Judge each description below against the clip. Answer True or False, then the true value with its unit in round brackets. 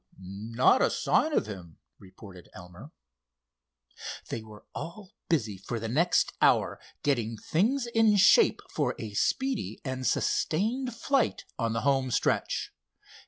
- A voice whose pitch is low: True (130 Hz)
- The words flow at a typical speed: False (130 wpm)